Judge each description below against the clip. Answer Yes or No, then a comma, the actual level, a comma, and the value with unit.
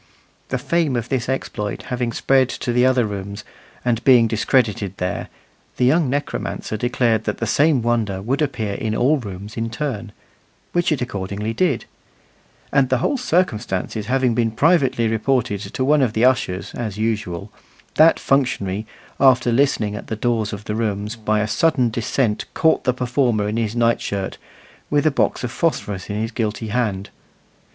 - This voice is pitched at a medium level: No, low, 115 Hz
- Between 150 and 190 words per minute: Yes, average, 175 wpm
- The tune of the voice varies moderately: Yes, average, 3.7 semitones